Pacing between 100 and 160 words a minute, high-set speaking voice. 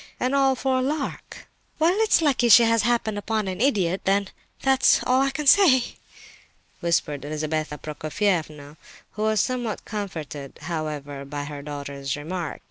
Yes: average, 150 wpm; high, 195 Hz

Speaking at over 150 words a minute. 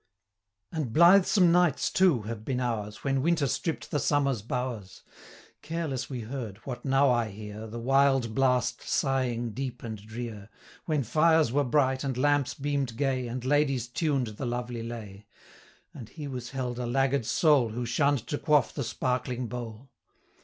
Yes: average, 165 wpm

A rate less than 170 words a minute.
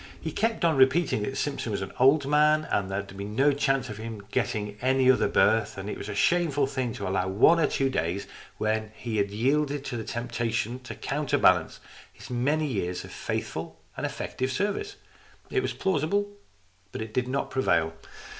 No: average, 195 wpm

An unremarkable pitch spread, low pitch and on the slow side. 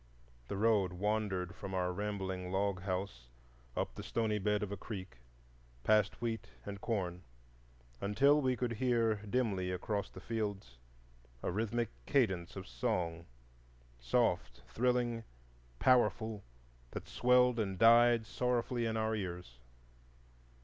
Yes: average, 3.9 semitones; low, 105 Hz; slow, 120 wpm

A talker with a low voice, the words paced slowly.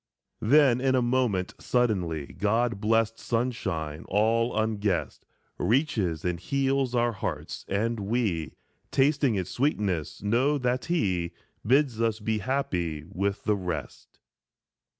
Yes: low, 110 Hz; slow, 120 wpm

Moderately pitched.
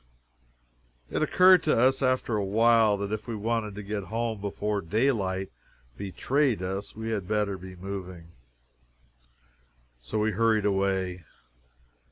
No: low, 105 Hz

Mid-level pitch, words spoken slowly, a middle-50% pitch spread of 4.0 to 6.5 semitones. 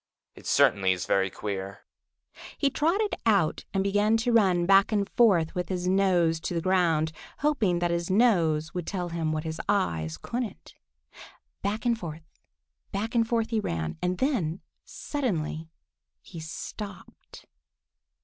No: medium, 180 Hz; average, 150 wpm; average, 5.2 semitones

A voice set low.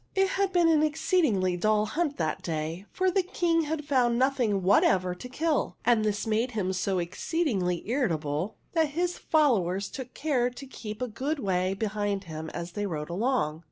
No: high, 220 Hz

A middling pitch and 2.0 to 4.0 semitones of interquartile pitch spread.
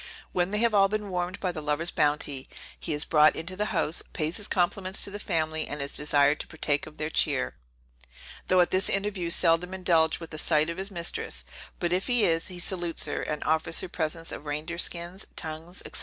Yes: medium, 170 Hz; average, 3.2 semitones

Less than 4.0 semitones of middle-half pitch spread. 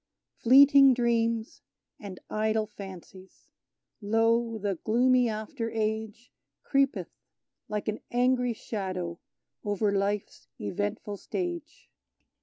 Yes: average, 3.1 semitones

